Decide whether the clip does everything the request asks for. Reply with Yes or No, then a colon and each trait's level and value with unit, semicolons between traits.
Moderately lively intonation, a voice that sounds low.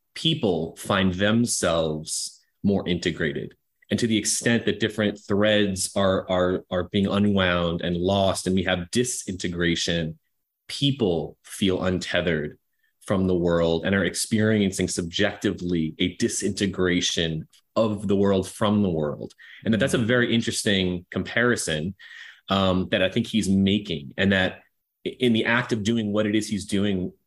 Yes: average, 3.0 semitones; very low, 95 Hz